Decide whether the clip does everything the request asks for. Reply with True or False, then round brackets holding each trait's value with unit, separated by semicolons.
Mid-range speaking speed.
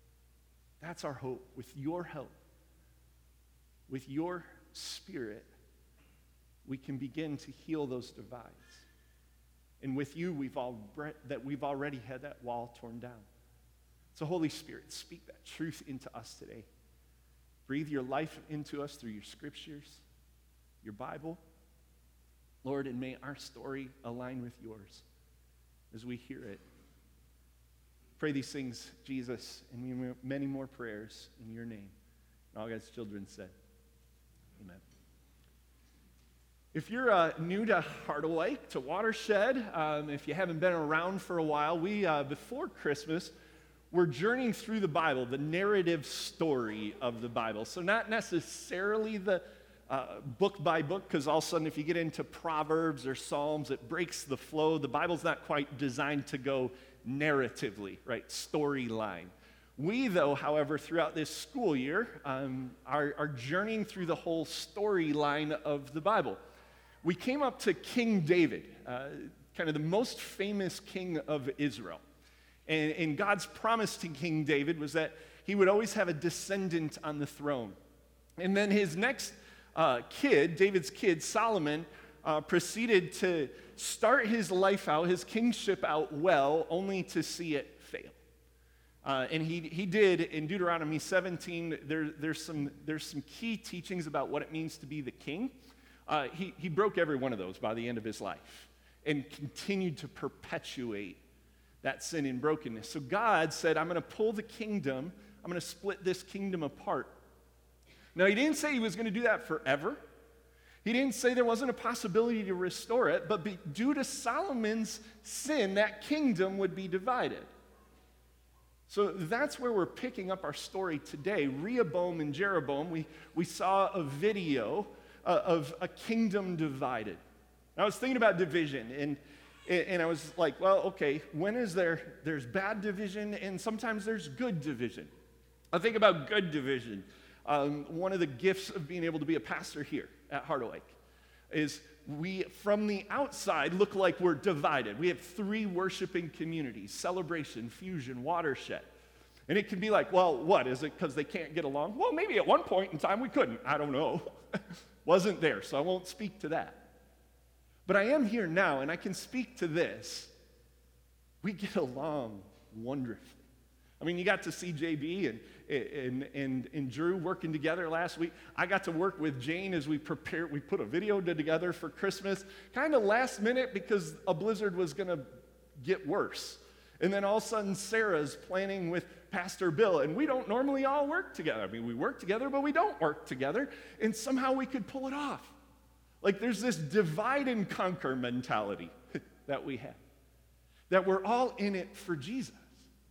True (170 wpm)